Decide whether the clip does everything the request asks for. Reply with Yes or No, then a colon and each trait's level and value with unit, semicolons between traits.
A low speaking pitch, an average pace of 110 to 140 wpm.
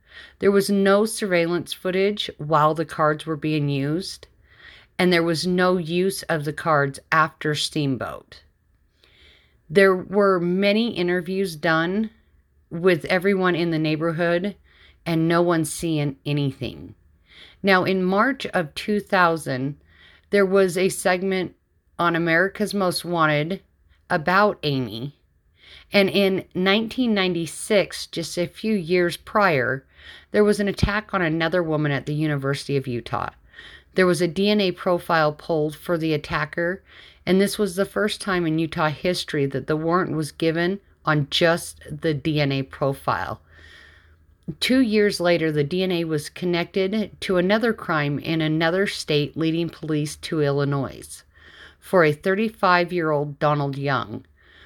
No: medium, 170 Hz; slow, 135 wpm